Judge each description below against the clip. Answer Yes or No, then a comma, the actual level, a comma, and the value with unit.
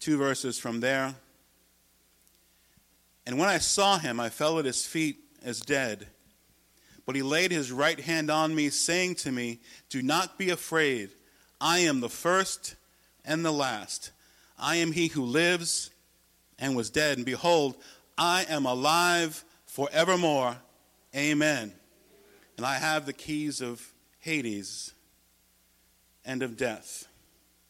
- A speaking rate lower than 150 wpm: Yes, slow, 135 wpm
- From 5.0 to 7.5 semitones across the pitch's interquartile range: Yes, wide, 5.5 semitones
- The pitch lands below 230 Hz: Yes, medium, 140 Hz